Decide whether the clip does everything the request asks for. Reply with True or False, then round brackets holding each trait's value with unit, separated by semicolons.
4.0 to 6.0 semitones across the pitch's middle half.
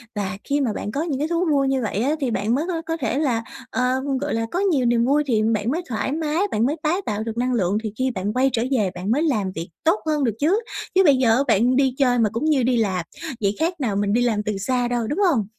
True (5.2 semitones)